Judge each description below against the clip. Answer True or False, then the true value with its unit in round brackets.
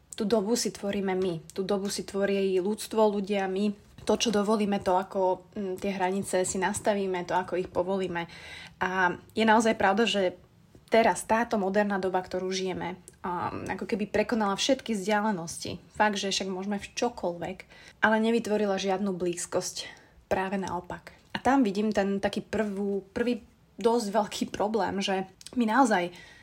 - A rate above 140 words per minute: True (150 wpm)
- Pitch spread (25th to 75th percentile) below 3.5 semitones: True (2.6 semitones)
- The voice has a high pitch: True (200 Hz)